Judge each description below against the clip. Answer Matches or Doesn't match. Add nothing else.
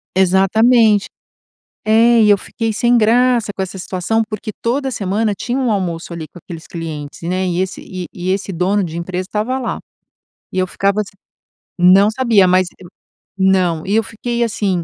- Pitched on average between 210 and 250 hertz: Doesn't match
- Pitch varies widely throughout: Doesn't match